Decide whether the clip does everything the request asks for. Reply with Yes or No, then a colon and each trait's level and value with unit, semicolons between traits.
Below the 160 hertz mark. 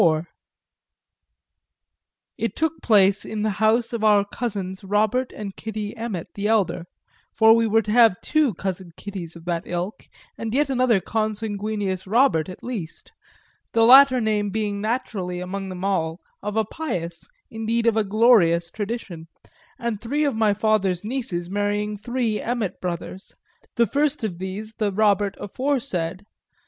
No: high, 210 Hz